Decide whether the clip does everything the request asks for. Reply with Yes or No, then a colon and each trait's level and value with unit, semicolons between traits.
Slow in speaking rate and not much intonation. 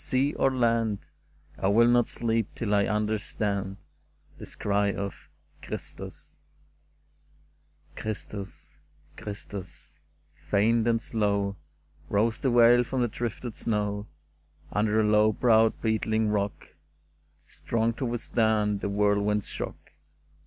Yes: slow, 125 wpm; narrow, 2.2 semitones